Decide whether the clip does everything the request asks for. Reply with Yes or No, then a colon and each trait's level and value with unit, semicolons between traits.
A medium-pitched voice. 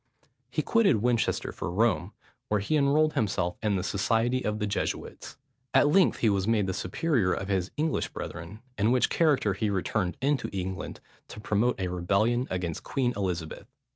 No: low, 105 Hz